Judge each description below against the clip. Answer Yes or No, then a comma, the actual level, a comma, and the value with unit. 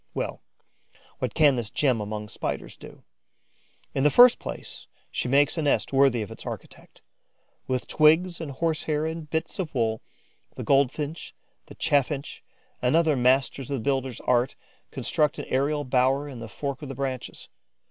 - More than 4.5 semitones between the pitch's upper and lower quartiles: No, average, 3.1 semitones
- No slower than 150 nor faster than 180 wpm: Yes, average, 170 wpm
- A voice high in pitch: No, medium, 140 Hz